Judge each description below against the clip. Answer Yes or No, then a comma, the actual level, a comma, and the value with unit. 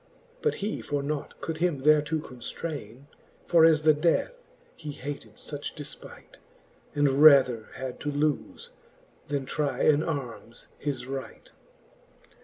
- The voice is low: No, medium, 145 Hz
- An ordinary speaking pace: No, slow, 130 wpm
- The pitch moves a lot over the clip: No, narrow, 2.6 semitones